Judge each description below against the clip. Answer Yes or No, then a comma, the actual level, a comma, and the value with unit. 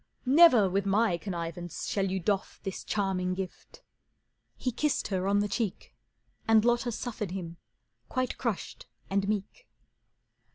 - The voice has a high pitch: Yes, high, 200 Hz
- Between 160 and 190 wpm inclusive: No, slow, 135 wpm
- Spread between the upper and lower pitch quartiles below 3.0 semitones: No, average, 3.7 semitones